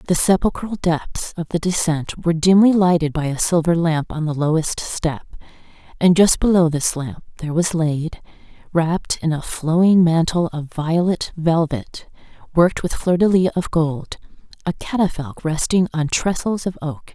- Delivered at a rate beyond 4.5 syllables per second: Yes, 4.7 syllables/s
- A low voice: No, medium, 165 Hz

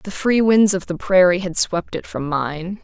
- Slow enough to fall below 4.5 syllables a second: Yes, 4.3 syllables/s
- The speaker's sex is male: No, female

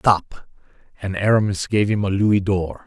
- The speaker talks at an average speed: Yes, average, 170 wpm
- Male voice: Yes, male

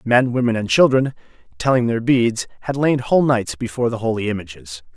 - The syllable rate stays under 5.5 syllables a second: No, 5.8 syllables/s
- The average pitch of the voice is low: Yes, low, 115 Hz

